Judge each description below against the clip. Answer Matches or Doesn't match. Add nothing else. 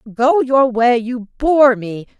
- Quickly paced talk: Doesn't match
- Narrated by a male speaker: Doesn't match